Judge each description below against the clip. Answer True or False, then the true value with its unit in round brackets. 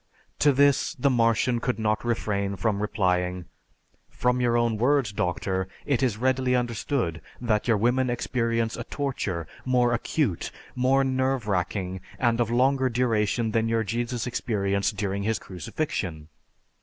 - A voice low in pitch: True (115 Hz)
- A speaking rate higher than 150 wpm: False (145 wpm)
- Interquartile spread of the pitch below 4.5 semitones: True (4.0 semitones)